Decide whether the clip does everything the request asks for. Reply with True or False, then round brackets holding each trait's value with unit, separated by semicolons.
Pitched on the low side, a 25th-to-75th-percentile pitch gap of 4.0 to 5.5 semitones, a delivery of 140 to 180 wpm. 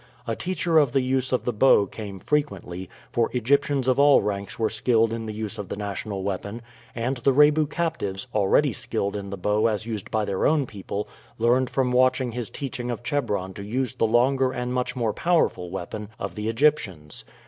False (115 Hz; 4.3 semitones; 200 wpm)